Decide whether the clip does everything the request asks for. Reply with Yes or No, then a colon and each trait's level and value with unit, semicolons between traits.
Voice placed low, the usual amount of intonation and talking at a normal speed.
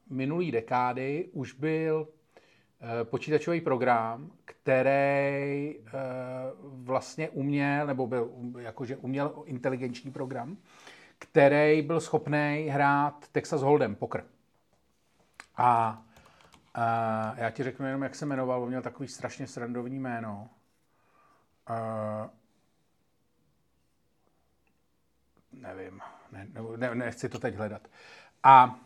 No: low, 130 Hz; average, 3.0 semitones; slow, 105 wpm